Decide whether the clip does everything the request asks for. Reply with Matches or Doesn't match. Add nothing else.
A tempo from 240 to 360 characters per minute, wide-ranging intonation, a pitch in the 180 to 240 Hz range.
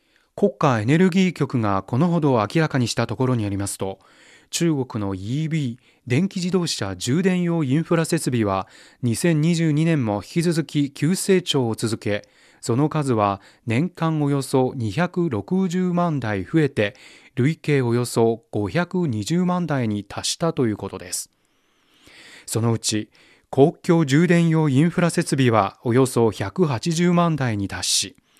Doesn't match